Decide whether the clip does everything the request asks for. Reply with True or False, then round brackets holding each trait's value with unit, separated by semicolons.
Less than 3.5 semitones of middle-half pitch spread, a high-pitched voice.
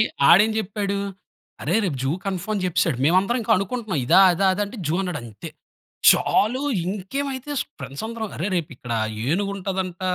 False (3.8 semitones; 195 Hz)